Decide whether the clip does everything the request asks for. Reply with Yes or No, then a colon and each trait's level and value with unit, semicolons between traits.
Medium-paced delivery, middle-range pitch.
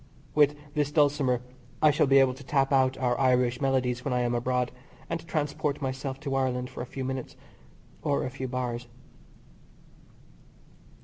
No: average, 165 wpm; low, 130 Hz